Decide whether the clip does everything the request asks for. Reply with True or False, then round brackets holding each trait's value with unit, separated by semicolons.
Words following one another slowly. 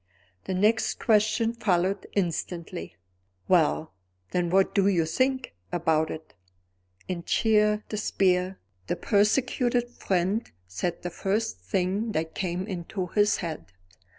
True (120 wpm)